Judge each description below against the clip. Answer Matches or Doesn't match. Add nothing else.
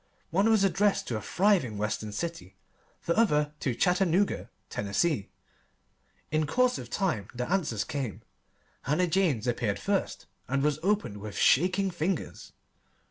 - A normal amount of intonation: Doesn't match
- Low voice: Doesn't match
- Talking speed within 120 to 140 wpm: Matches